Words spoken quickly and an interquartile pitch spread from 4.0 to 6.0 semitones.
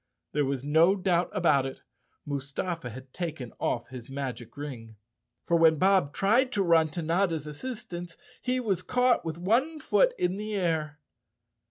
No: average, 160 wpm; wide, 5.6 semitones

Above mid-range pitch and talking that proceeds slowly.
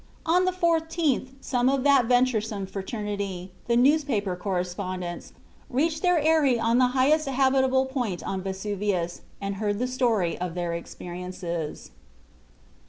Yes: high, 230 Hz; slow, 130 wpm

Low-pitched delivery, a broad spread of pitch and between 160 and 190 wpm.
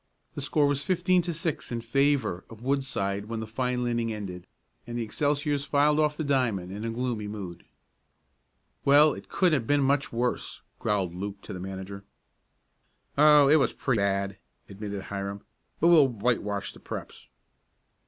Yes: low, 120 Hz; wide, 6.1 semitones; average, 165 wpm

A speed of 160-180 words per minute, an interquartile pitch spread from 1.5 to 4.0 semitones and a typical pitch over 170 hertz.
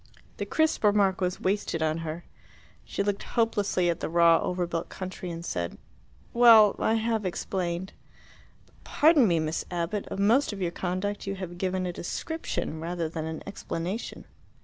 Yes: average, 170 wpm; average, 3.3 semitones; medium, 185 Hz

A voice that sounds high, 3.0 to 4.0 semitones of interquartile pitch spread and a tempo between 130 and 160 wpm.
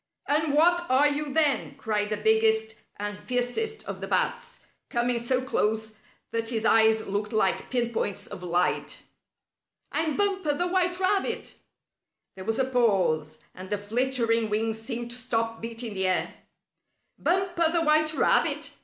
No: high, 235 Hz; wide, 5.4 semitones; average, 155 wpm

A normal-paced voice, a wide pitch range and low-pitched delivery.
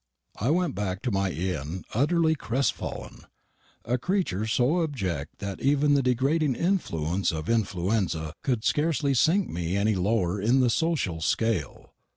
Yes: average, 145 wpm; wide, 7.6 semitones; low, 115 Hz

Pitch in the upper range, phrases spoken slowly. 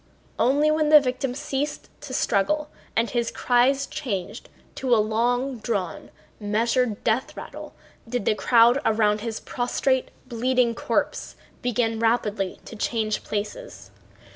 Yes: high, 240 Hz; slow, 130 wpm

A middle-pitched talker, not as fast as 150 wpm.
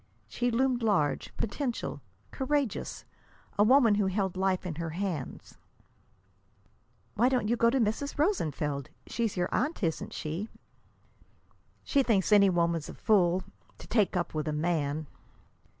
No: high, 200 Hz; average, 140 wpm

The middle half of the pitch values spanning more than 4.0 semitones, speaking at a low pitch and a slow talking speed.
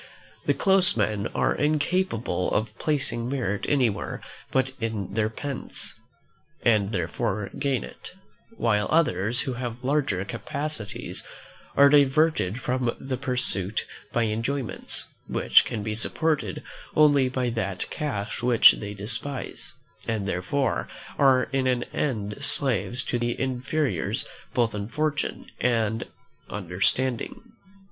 Yes: average, 4.9 semitones; low, 120 Hz; slow, 120 wpm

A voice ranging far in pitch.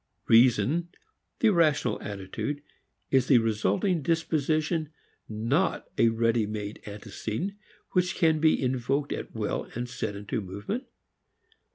Yes: wide, 6.7 semitones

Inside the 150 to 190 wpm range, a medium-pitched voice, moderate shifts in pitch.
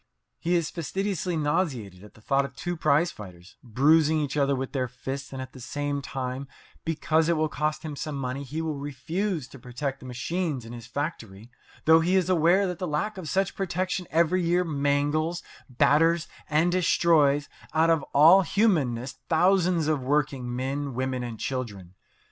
Yes: average, 175 wpm; medium, 150 Hz; average, 4.3 semitones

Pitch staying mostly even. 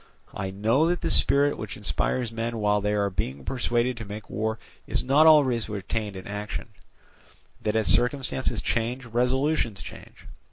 No: average, 3.6 semitones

